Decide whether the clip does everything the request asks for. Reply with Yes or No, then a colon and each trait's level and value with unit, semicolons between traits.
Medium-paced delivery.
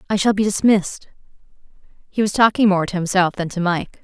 Yes: average, 195 wpm